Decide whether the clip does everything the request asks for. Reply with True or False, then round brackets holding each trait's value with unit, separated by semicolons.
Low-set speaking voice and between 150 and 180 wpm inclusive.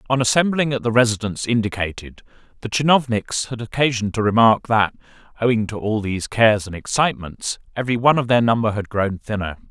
True (115 Hz; 175 wpm)